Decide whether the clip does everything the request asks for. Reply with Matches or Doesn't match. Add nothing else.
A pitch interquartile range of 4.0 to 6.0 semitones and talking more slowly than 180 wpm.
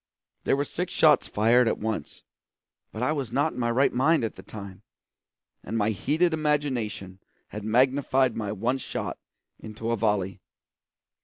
Matches